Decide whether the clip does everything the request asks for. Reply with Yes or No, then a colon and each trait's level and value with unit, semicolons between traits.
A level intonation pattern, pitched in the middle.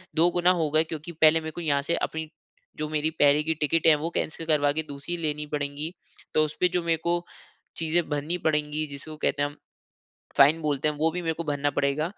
Yes: narrow, 1.8 semitones; medium, 155 Hz